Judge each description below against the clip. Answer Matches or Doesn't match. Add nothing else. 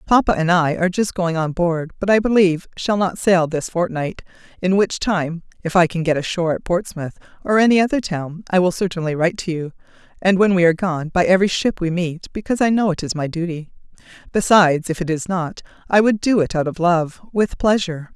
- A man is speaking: Doesn't match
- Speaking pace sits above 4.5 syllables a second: Matches